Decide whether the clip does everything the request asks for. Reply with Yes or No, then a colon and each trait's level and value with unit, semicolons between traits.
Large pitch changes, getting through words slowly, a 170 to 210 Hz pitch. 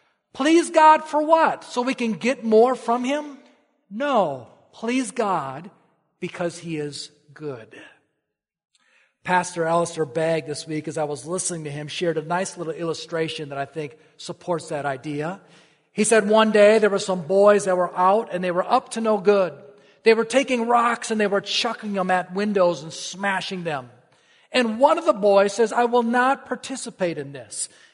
No: wide, 6.4 semitones; average, 180 wpm; high, 190 Hz